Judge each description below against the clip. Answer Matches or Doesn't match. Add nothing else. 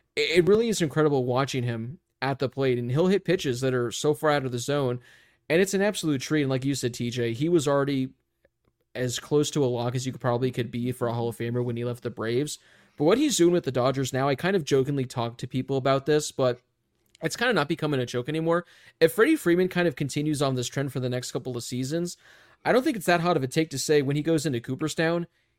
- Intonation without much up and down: Doesn't match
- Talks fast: Matches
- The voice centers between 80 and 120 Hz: Doesn't match